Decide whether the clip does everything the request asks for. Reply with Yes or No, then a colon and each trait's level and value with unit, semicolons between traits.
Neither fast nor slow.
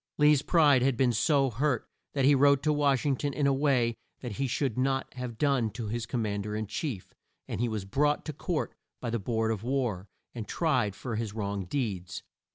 No: fast, 220 wpm